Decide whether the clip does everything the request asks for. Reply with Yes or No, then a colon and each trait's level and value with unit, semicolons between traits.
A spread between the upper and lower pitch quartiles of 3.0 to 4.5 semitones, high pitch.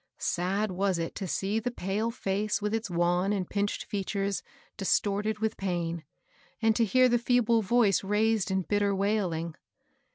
No: narrow, 2.5 semitones; high, 200 Hz